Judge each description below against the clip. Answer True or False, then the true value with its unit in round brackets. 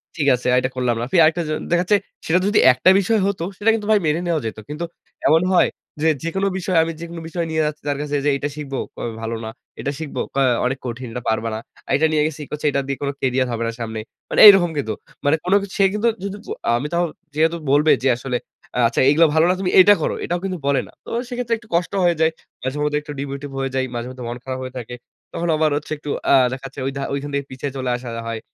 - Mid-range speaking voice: True (150 Hz)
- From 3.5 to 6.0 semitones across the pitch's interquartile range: True (4.8 semitones)